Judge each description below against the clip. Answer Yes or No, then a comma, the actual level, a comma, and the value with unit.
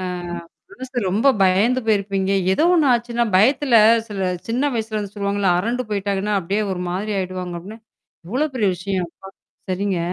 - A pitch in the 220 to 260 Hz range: No, high, 205 Hz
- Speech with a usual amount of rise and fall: Yes, average, 3.7 semitones